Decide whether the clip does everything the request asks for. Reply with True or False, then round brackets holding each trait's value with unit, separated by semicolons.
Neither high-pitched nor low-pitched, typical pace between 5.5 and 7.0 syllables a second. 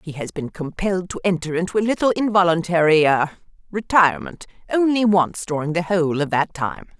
True (175 Hz; 5.7 syllables/s)